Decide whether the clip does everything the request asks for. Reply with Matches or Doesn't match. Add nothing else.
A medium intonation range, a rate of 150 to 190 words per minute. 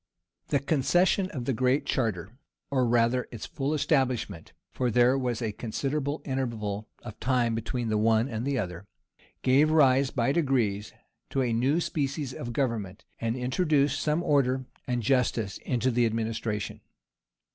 Matches